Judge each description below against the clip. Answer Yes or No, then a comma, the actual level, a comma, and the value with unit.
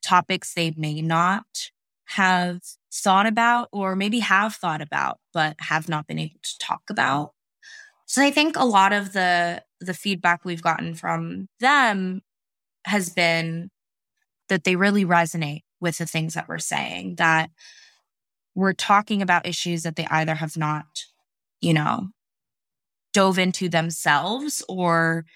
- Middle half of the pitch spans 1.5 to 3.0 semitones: No, average, 3.8 semitones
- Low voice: No, medium, 175 Hz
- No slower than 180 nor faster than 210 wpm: No, average, 145 wpm